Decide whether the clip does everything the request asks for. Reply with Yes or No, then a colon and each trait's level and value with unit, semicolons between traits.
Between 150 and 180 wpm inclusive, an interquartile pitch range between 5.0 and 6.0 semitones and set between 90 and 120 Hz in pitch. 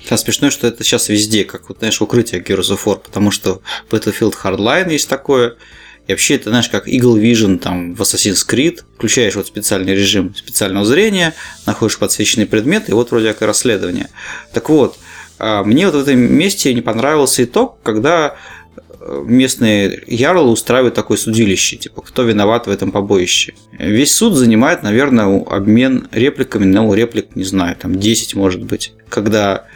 No: fast, 160 wpm; average, 3.2 semitones; low, 110 Hz